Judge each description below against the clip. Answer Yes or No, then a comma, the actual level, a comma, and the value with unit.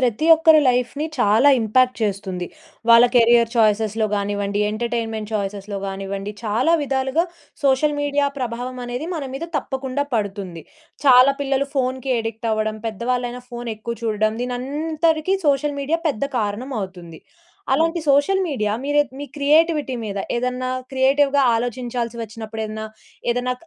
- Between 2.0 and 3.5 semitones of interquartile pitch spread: No, average, 4.3 semitones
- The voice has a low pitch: No, high, 245 Hz